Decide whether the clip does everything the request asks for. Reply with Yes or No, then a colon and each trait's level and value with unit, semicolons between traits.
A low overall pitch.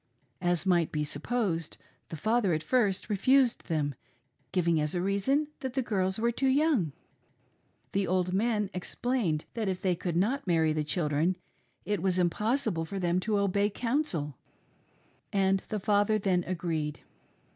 No: high, 190 Hz